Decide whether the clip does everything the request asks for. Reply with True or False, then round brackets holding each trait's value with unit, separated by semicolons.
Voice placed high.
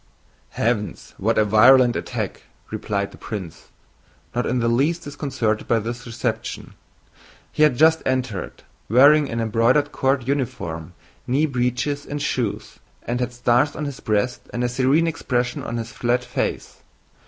False (125 Hz)